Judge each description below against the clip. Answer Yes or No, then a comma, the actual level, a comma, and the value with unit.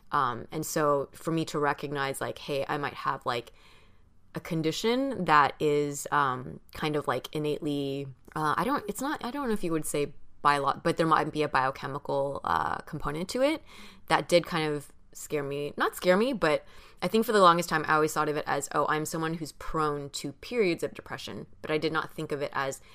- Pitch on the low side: No, medium, 150 Hz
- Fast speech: Yes, fast, 220 wpm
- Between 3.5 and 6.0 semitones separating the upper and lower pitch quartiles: No, narrow, 2.5 semitones